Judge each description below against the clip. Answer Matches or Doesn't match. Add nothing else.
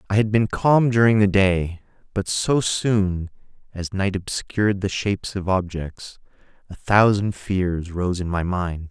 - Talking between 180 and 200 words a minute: Doesn't match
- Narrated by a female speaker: Doesn't match